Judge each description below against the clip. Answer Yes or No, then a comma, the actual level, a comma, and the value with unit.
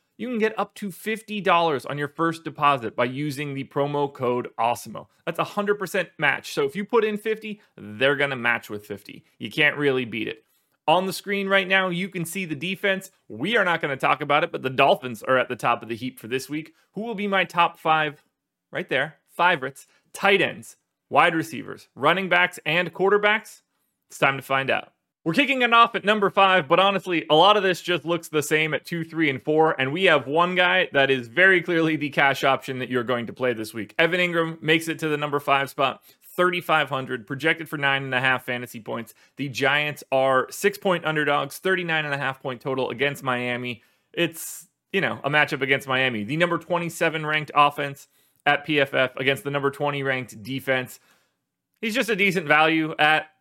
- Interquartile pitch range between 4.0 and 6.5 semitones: Yes, average, 5.1 semitones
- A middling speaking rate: No, fast, 210 wpm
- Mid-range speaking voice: Yes, medium, 150 Hz